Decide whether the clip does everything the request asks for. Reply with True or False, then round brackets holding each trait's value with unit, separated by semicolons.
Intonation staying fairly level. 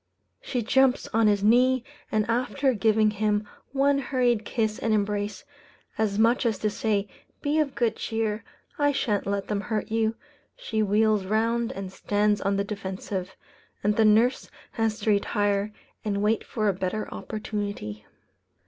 True (2.1 semitones)